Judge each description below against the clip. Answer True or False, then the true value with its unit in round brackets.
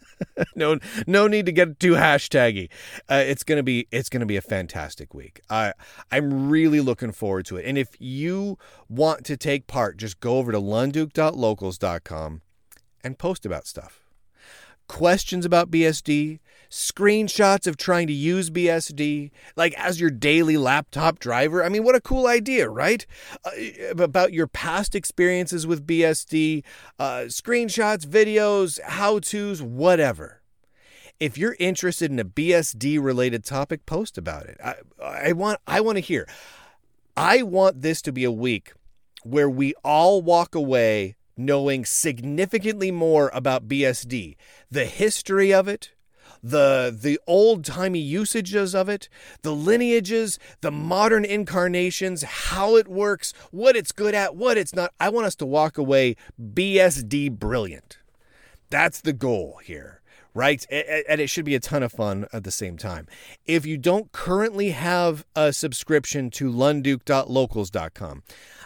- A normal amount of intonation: False (6.1 semitones)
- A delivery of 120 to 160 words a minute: True (150 wpm)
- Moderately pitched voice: True (155 Hz)